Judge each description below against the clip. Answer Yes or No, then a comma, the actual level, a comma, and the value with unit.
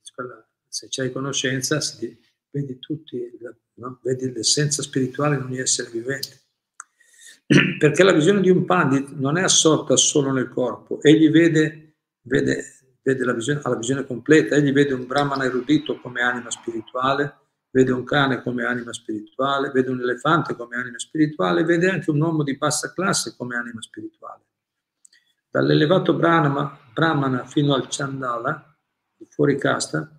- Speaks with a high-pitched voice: No, medium, 140 Hz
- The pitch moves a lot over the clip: No, average, 3.5 semitones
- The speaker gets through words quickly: No, average, 145 wpm